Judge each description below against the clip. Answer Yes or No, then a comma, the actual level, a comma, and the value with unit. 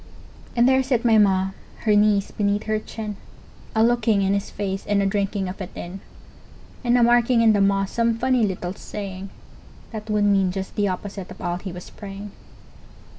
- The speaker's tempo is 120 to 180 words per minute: No, average, 190 wpm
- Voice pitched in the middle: No, high, 205 Hz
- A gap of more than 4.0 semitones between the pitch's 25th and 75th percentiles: No, narrow, 2.4 semitones